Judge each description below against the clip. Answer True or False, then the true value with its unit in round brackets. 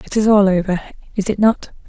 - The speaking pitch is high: True (200 Hz)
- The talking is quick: True (225 wpm)